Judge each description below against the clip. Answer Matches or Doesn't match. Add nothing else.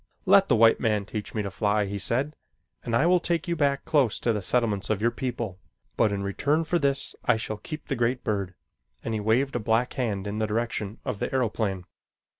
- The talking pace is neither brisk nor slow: Doesn't match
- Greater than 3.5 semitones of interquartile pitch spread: Matches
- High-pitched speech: Doesn't match